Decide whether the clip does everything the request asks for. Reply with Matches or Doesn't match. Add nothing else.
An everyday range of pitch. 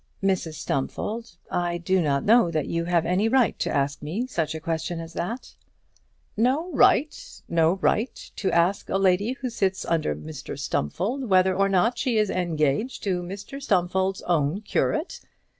Matches